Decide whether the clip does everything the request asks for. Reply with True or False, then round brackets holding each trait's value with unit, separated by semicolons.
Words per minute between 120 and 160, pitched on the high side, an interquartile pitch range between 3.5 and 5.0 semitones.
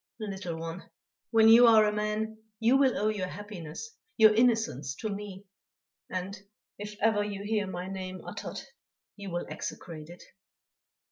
False (150 wpm; 205 Hz; 2.9 semitones)